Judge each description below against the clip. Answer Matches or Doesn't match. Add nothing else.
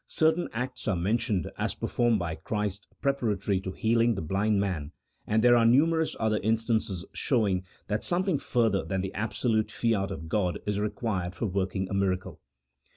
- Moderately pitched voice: Doesn't match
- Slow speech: Doesn't match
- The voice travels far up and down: Doesn't match